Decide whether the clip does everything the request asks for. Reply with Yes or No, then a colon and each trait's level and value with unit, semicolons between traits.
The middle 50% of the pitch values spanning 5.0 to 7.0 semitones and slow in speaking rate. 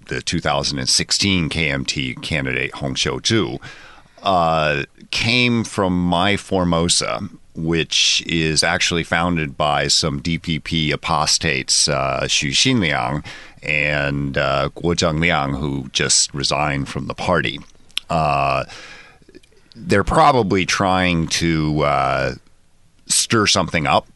No: average, 3.2 semitones; slow, 100 wpm